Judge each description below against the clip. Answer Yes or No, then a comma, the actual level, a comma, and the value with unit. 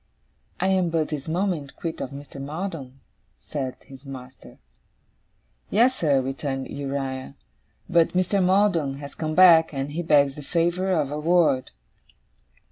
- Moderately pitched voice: Yes, medium, 150 Hz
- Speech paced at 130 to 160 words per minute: Yes, average, 140 wpm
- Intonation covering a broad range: No, average, 4.2 semitones